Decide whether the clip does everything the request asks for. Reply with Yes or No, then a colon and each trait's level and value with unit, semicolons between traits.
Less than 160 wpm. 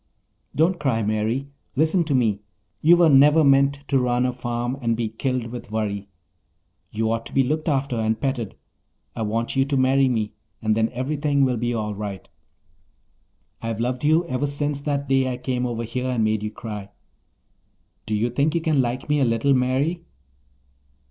No: average, 185 wpm